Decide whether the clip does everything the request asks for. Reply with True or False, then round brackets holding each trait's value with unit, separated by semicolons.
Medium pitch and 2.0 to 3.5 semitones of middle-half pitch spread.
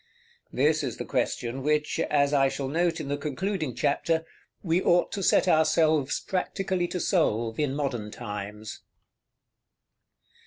False (150 Hz; 4.1 semitones)